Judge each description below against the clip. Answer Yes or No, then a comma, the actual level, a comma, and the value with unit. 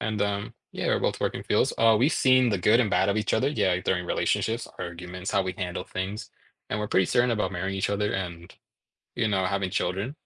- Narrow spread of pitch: No, average, 3.2 semitones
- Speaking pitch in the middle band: No, low, 100 Hz